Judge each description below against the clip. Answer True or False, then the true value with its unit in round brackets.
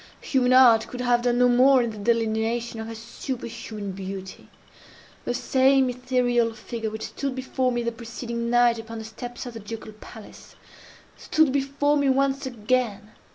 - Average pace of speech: True (165 wpm)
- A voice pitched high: True (240 Hz)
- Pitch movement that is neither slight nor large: False (2.3 semitones)